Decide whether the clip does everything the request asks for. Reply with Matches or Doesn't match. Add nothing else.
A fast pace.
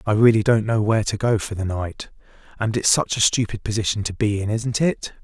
Matches